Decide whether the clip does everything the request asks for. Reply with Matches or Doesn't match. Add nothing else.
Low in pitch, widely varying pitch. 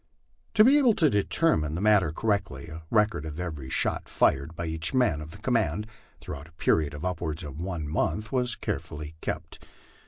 Matches